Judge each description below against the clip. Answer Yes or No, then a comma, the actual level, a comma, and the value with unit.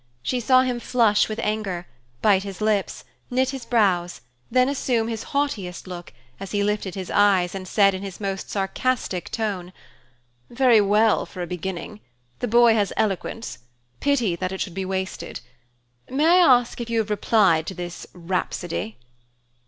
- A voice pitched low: No, high, 205 Hz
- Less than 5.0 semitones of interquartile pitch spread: Yes, average, 4.0 semitones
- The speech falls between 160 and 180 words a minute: Yes, average, 170 wpm